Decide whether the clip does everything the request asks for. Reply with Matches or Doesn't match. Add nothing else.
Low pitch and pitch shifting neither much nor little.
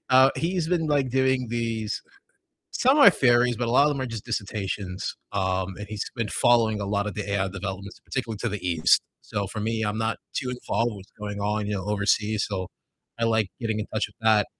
Matches